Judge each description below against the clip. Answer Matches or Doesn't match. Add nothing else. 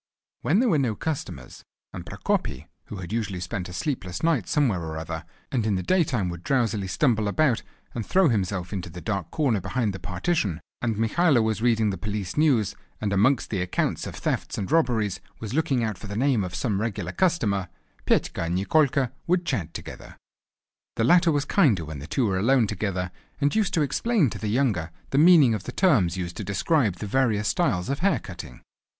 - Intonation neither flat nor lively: Doesn't match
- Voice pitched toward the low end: Matches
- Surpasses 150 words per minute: Matches